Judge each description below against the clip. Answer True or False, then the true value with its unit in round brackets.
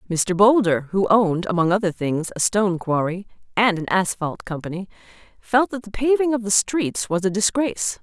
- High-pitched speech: True (200 Hz)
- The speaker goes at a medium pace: True (180 wpm)